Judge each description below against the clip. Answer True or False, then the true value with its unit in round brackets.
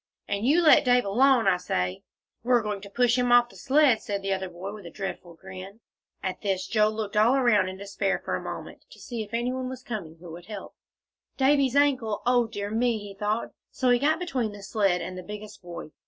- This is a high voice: True (215 Hz)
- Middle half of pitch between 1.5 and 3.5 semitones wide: False (4.2 semitones)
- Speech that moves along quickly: True (230 wpm)